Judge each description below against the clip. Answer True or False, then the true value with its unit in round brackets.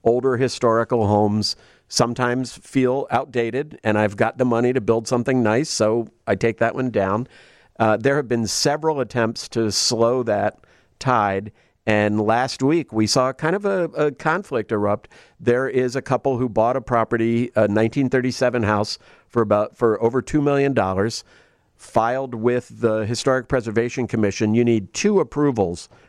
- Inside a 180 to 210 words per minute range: False (160 wpm)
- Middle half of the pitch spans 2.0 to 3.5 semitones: True (3.1 semitones)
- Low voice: True (120 Hz)